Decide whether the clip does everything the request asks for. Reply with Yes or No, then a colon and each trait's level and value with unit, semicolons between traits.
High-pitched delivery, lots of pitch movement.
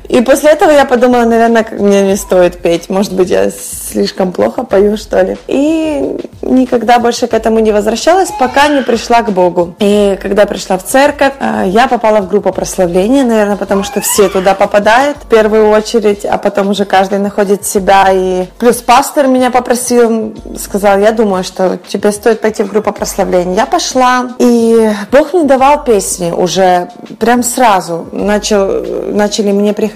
No: high, 215 Hz; average, 3.8 semitones